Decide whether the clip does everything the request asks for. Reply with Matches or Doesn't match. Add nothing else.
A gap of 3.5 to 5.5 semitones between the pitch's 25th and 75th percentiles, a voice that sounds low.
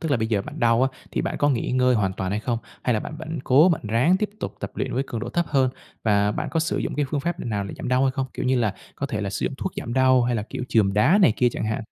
Matches